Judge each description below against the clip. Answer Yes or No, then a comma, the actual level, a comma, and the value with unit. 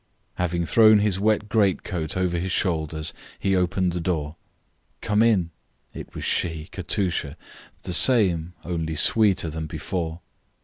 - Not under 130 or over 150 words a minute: Yes, slow, 135 wpm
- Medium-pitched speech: No, very low, 90 Hz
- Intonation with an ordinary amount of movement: Yes, average, 3.4 semitones